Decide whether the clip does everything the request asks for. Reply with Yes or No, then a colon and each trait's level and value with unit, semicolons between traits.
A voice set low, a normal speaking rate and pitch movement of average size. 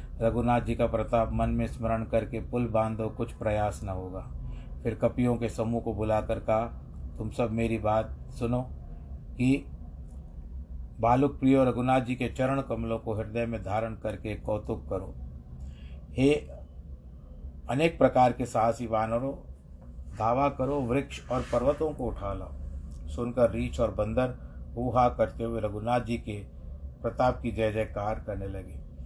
No: low, 110 Hz; average, 150 wpm; wide, 8.0 semitones